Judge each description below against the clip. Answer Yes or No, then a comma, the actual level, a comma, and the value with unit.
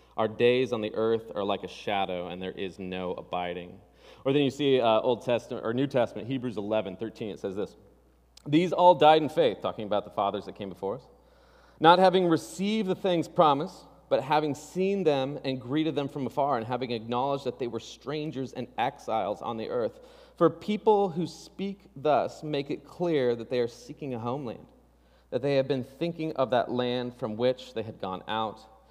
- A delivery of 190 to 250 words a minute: Yes, average, 200 wpm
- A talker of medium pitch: No, low, 130 Hz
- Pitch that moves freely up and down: Yes, wide, 6.1 semitones